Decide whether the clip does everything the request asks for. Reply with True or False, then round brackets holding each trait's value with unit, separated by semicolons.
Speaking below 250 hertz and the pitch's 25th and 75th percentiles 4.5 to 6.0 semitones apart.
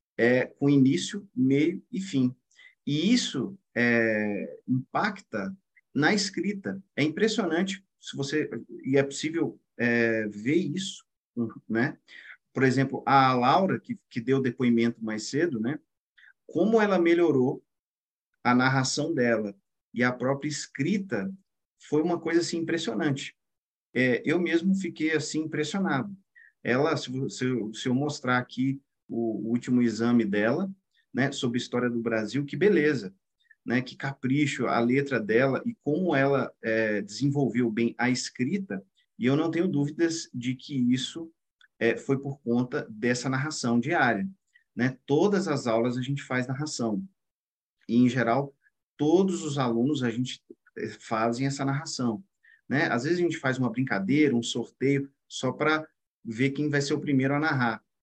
True (135 Hz; 5.1 semitones)